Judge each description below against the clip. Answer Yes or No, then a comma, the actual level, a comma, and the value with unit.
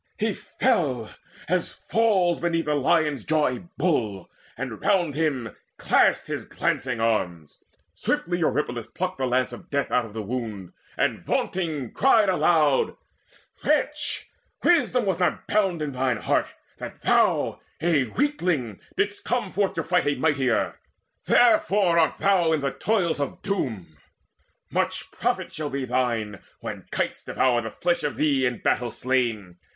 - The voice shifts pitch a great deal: Yes, wide, 6.8 semitones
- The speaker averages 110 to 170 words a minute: Yes, average, 150 wpm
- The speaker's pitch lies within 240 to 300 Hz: No, medium, 150 Hz